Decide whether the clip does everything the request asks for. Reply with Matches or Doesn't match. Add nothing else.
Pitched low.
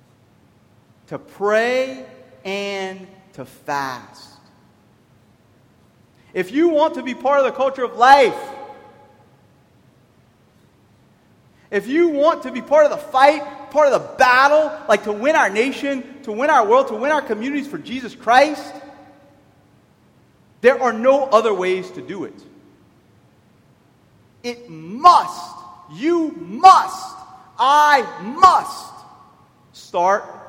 Doesn't match